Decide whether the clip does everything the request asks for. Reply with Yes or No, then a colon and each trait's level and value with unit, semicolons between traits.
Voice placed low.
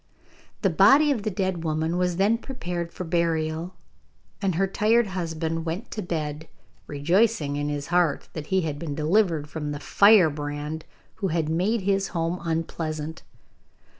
No: medium, 170 Hz